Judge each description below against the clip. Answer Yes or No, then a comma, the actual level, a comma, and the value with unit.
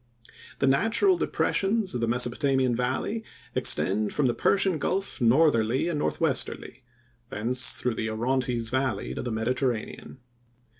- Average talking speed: No, slow, 130 wpm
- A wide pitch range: No, average, 4.3 semitones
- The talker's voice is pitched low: Yes, low, 130 Hz